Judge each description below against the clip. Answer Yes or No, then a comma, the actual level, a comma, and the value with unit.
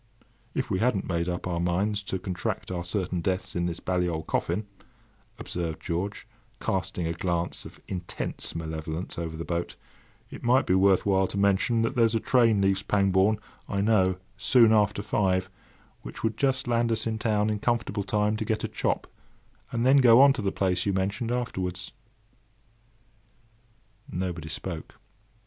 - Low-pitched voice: Yes, very low, 95 Hz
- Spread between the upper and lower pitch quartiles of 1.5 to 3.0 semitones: No, average, 3.7 semitones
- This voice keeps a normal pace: Yes, average, 170 wpm